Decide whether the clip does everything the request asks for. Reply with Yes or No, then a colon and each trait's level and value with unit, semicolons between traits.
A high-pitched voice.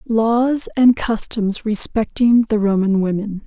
Yes: high, 220 Hz